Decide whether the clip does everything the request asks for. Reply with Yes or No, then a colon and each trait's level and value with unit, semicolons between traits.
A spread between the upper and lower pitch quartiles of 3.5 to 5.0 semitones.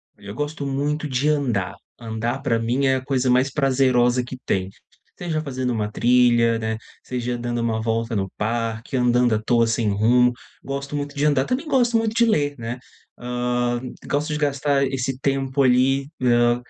No: average, 2.9 semitones